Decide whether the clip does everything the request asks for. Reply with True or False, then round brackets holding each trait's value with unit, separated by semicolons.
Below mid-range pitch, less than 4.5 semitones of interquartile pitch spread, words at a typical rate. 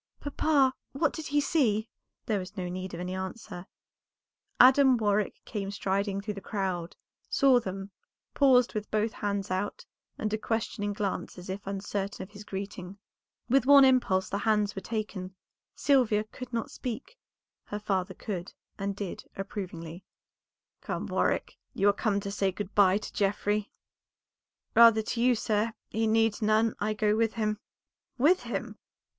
False (210 Hz; 2.8 semitones; 160 wpm)